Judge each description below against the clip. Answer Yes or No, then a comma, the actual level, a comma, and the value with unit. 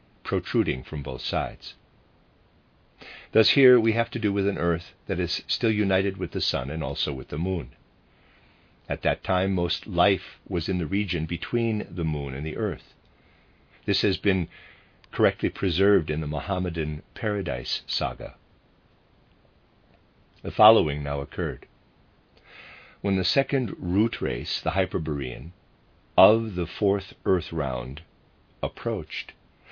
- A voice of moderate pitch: No, very low, 90 Hz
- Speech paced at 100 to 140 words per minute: Yes, slow, 135 wpm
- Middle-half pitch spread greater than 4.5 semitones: No, average, 4.2 semitones